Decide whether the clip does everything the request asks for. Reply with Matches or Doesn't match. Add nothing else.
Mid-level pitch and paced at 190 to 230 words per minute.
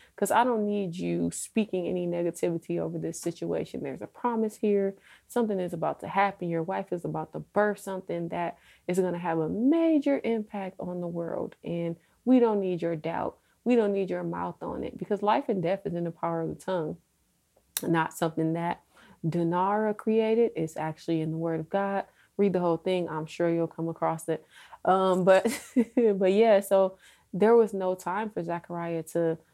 Matches